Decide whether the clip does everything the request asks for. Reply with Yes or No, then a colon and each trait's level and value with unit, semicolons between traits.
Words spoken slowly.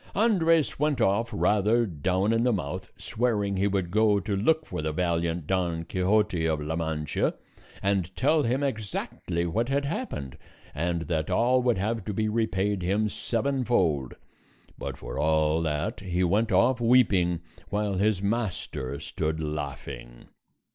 No: average, 150 wpm